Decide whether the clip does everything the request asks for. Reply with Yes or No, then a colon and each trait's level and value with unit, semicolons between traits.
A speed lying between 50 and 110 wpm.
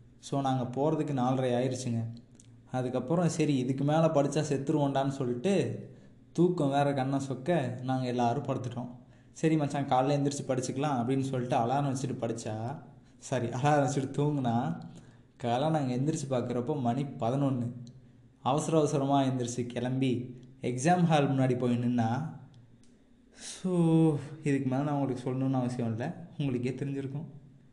No: average, 125 wpm